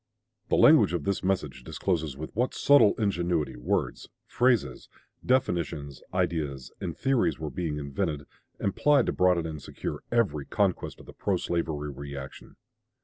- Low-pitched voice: Yes, very low, 80 Hz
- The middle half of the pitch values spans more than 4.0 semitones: Yes, average, 5.3 semitones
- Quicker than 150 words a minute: No, average, 145 wpm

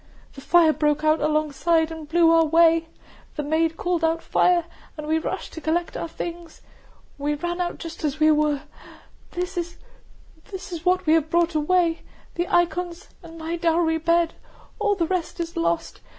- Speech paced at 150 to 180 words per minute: Yes, average, 170 wpm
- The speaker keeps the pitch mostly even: Yes, narrow, 1.8 semitones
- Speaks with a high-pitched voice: Yes, very high, 330 Hz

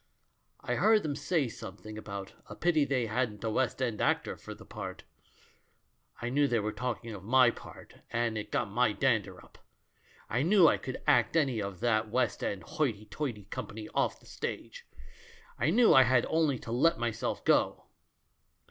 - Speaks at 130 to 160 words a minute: No, average, 180 wpm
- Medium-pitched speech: No, low, 120 Hz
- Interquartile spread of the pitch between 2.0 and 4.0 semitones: No, average, 4.5 semitones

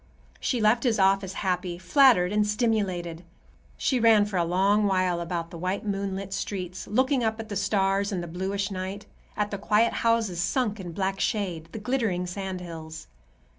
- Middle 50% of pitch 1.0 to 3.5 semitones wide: Yes, average, 2.9 semitones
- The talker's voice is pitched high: Yes, high, 195 Hz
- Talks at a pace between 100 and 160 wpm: No, average, 175 wpm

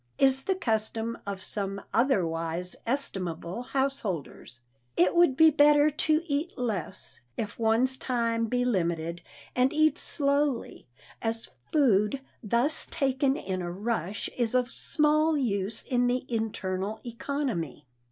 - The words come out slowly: Yes, slow, 125 wpm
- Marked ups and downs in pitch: Yes, wide, 5.9 semitones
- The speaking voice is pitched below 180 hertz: No, high, 235 Hz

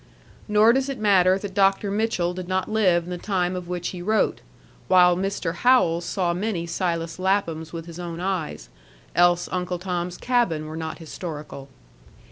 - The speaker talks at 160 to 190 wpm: Yes, average, 170 wpm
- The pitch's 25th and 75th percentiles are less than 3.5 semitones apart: Yes, narrow, 2.4 semitones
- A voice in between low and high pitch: Yes, medium, 180 Hz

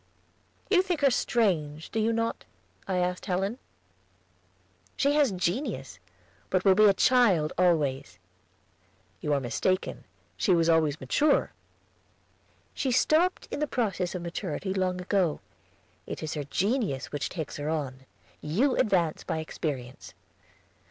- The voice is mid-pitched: Yes, medium, 180 Hz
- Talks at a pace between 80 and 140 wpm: Yes, slow, 135 wpm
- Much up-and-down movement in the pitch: Yes, wide, 6.7 semitones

